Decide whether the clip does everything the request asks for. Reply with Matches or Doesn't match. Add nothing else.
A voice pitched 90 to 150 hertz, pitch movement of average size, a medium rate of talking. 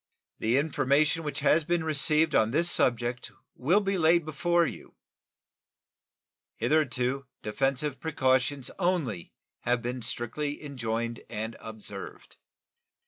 Doesn't match